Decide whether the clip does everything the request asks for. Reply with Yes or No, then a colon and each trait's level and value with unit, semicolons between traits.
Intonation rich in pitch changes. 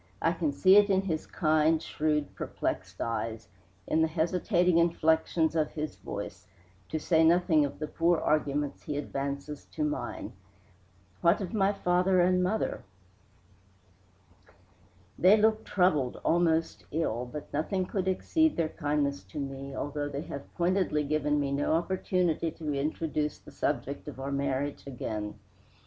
No: average, 3.6 semitones